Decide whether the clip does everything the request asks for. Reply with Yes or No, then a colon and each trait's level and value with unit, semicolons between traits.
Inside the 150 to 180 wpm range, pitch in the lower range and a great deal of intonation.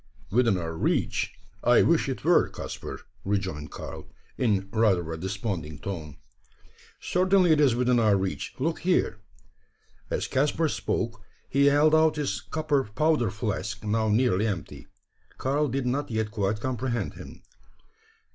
No: average, 140 wpm; low, 115 Hz; wide, 6.3 semitones